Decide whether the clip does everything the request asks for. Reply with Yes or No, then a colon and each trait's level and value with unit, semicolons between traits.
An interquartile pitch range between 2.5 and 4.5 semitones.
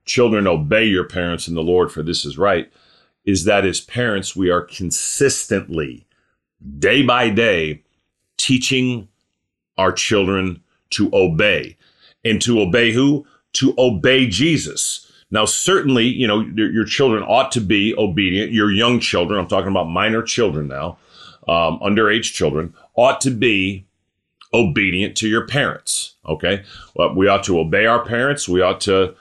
No: average, 4.9 semitones